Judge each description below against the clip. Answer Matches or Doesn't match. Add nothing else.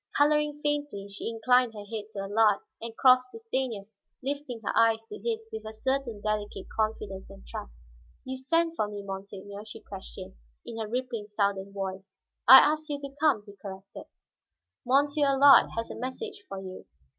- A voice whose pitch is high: Matches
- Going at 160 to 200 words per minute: Matches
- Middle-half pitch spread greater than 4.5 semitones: Matches